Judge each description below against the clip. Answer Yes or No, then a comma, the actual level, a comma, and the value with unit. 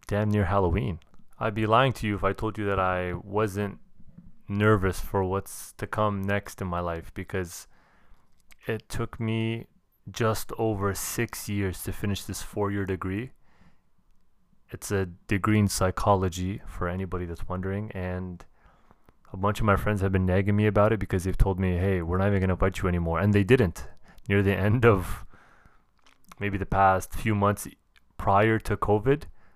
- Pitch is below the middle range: Yes, low, 100 Hz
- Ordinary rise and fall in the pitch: No, narrow, 2.1 semitones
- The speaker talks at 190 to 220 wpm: No, average, 175 wpm